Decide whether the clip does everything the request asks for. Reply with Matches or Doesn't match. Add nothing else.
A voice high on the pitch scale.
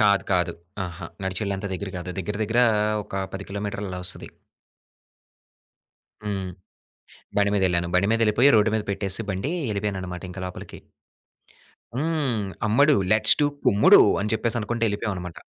Doesn't match